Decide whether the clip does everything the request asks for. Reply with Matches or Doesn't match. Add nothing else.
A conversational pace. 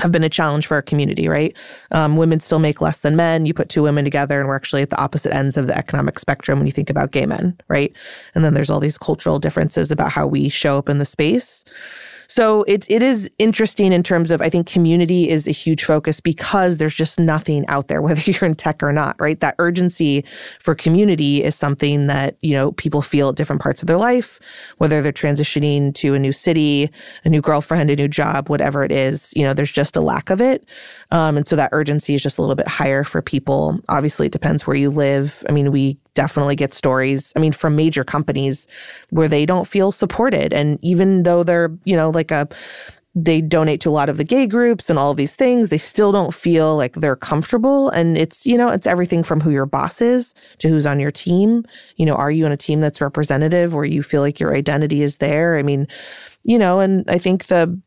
Doesn't match